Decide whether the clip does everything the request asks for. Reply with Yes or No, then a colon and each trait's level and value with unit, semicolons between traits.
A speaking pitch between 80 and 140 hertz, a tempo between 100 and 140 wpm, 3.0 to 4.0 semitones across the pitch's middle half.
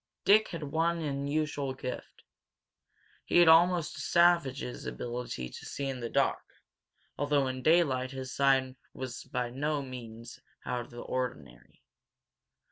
Yes: low, 135 Hz; slow, 135 wpm; average, 3.4 semitones